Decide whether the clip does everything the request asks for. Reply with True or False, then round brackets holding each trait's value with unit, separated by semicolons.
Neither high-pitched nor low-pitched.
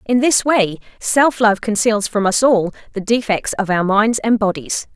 False (215 Hz)